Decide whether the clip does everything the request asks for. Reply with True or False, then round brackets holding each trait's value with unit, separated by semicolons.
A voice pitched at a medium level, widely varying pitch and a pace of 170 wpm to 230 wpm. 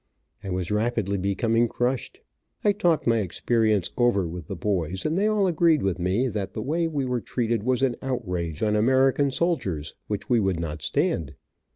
False (115 Hz; 5.9 semitones; 185 wpm)